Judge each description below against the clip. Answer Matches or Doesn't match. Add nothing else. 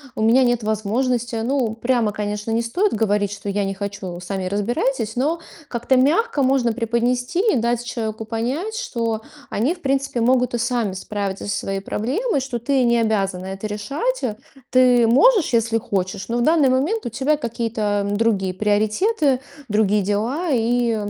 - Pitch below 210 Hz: Doesn't match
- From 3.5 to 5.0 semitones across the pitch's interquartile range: Matches